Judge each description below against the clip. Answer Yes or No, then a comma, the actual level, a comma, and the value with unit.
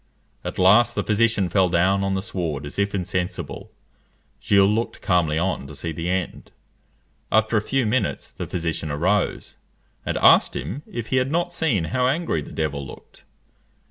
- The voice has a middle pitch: No, very low, 95 Hz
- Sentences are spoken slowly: No, average, 175 wpm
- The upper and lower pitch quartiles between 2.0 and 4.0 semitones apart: No, average, 5.0 semitones